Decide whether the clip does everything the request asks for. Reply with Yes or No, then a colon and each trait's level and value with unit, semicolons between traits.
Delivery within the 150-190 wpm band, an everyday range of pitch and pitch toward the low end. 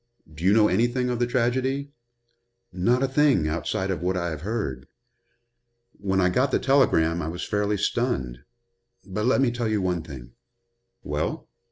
No: average, 170 wpm; wide, 6.4 semitones; low, 100 Hz